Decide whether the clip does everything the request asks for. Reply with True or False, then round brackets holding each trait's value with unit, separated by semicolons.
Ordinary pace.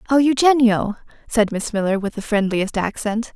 True (160 wpm)